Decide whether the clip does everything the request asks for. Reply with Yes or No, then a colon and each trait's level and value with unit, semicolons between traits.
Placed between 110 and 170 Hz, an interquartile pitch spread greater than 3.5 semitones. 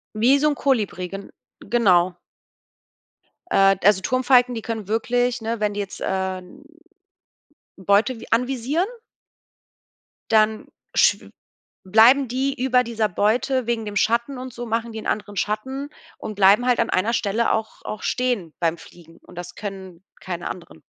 No: high, 220 Hz; average, 4.1 semitones